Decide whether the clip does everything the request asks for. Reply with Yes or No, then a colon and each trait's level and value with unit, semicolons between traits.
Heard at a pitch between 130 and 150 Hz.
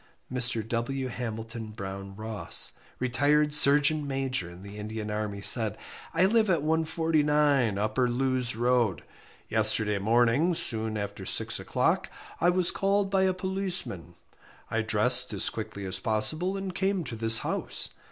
No: low, 120 Hz